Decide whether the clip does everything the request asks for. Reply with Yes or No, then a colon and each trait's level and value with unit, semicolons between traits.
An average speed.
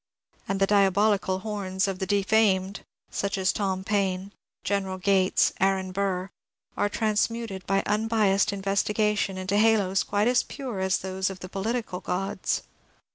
Yes: average, 155 wpm